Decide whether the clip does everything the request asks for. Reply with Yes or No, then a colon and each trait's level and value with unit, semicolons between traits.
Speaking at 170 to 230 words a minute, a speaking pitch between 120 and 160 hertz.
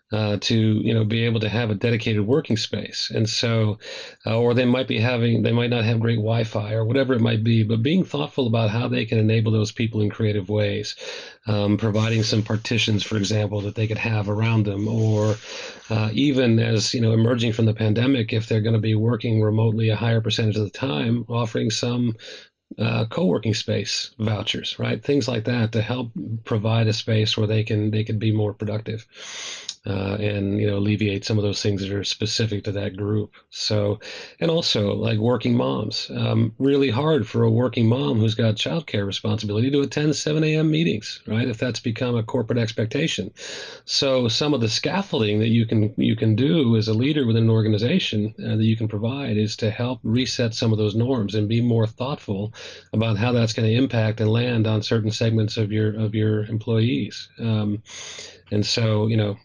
No: fast, 205 wpm; low, 110 Hz